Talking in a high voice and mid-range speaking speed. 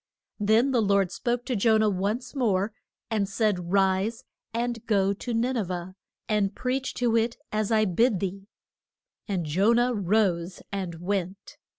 Yes: high, 210 Hz; average, 165 wpm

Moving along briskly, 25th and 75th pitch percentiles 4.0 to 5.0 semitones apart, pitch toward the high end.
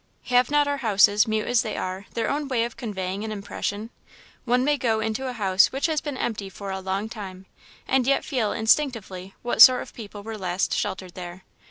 Yes: fast, 210 wpm; average, 4.4 semitones; high, 220 Hz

